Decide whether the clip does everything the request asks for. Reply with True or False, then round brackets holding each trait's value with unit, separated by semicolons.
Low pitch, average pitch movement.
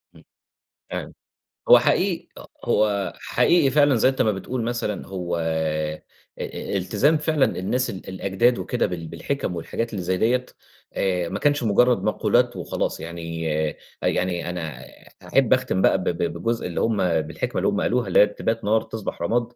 False (100 Hz; 5.9 semitones)